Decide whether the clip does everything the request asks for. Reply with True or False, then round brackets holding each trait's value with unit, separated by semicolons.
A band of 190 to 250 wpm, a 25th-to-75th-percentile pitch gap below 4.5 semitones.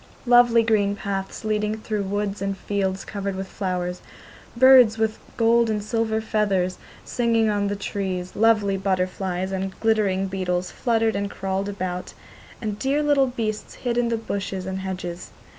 False (155 wpm; 2.8 semitones)